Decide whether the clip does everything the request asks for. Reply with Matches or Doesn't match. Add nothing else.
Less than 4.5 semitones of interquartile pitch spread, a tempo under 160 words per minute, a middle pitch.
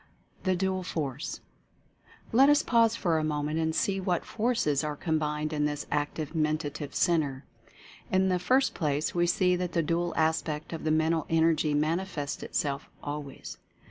Doesn't match